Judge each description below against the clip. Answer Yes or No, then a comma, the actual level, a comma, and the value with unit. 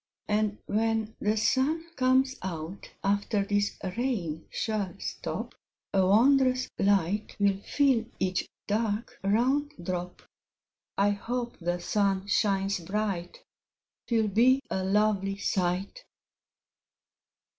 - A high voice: Yes, high, 205 Hz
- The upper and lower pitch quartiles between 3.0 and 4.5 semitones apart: Yes, average, 3.5 semitones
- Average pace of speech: No, slow, 105 wpm